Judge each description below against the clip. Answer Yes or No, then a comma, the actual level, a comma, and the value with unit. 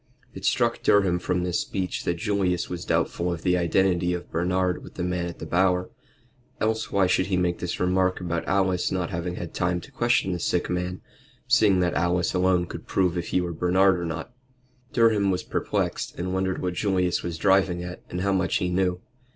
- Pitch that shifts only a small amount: Yes, narrow, 1.3 semitones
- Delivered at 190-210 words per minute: Yes, fast, 205 wpm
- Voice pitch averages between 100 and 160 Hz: No, very low, 90 Hz